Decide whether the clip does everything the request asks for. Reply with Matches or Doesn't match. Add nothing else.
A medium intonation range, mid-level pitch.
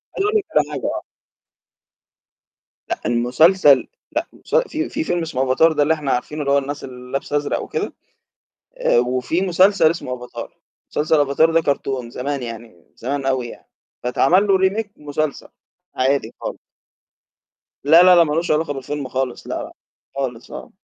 Matches